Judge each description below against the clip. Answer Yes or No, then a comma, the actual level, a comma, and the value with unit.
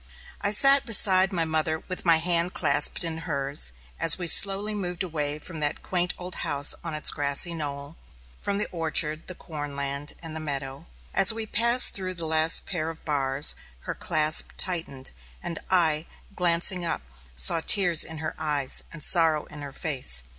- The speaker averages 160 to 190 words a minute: Yes, average, 175 wpm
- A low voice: No, medium, 160 Hz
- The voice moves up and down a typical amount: Yes, average, 3.4 semitones